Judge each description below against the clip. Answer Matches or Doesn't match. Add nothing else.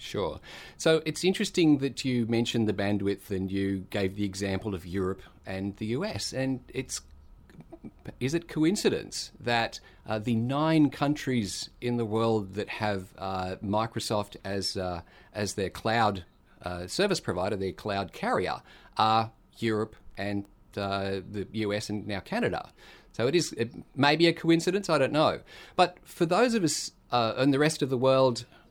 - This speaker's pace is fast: Doesn't match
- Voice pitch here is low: Matches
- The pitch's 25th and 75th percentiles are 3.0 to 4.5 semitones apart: Doesn't match